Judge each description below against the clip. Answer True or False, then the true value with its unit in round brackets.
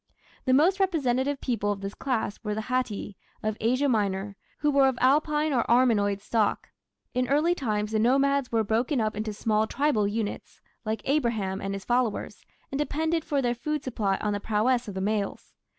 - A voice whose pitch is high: True (235 Hz)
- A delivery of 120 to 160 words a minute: False (185 wpm)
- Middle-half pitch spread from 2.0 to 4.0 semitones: False (4.7 semitones)